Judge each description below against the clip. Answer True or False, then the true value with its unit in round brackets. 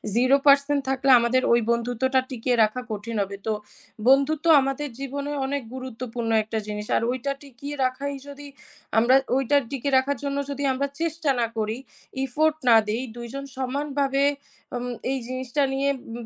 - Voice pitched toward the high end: True (265 Hz)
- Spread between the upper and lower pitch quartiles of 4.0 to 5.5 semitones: False (2.8 semitones)